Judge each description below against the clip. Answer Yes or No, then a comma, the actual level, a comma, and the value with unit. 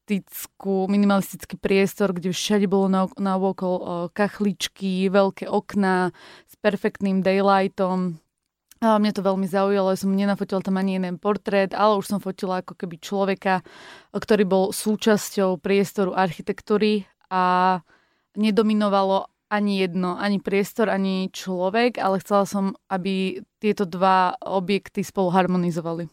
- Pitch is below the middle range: No, high, 195 Hz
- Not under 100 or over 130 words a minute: Yes, average, 125 wpm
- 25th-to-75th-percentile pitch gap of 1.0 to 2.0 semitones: Yes, narrow, 1.4 semitones